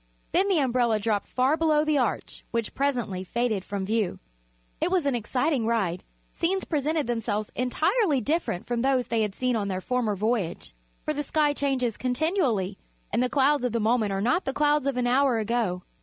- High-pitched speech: Yes, high, 245 Hz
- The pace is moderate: Yes, average, 190 wpm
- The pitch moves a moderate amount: Yes, average, 4.8 semitones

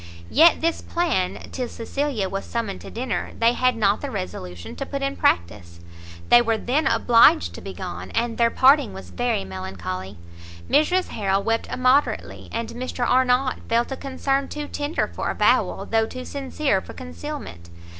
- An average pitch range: No, wide, 6.3 semitones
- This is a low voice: No, high, 235 Hz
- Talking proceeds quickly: No, average, 165 wpm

